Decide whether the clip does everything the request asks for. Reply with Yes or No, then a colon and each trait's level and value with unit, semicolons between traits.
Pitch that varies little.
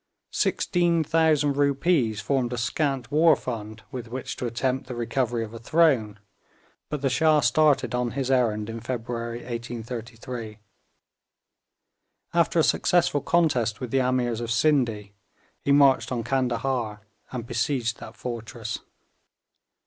No: average, 3.2 semitones